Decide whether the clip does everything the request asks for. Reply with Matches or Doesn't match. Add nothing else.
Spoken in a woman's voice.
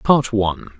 Doesn't match